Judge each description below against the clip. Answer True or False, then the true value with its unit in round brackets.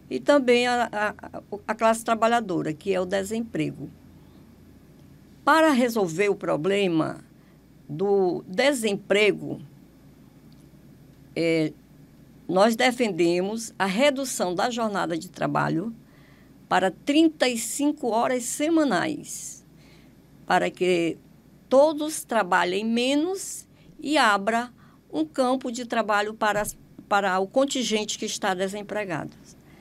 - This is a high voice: True (220 Hz)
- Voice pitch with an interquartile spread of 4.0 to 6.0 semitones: True (4.8 semitones)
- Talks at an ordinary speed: False (95 wpm)